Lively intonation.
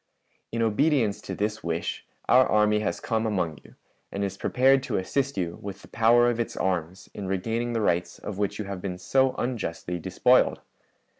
No: average, 4.0 semitones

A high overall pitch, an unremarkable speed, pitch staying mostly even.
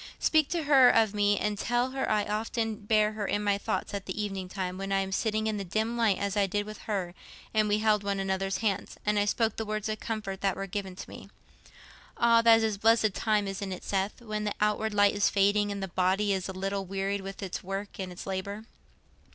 No: high, 205 Hz; fast, 240 wpm; narrow, 1.8 semitones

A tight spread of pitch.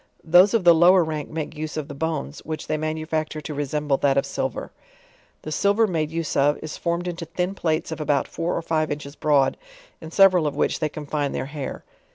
Yes: narrow, 2.2 semitones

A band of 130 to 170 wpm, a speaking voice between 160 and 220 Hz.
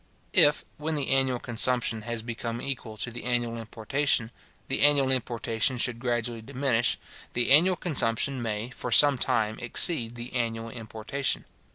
No: average, 150 wpm; low, 120 Hz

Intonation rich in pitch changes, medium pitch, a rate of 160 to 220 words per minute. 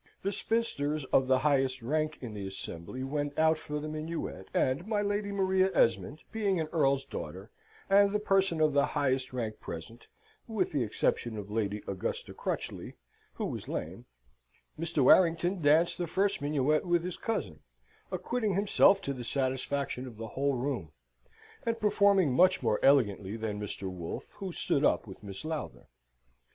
Yes: wide, 7.3 semitones; medium, 145 Hz; average, 165 wpm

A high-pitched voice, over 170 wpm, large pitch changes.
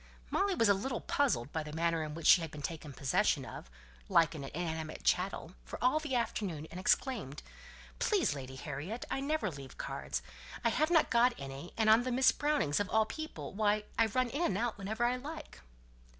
Yes: high, 205 Hz; fast, 205 wpm; wide, 8.1 semitones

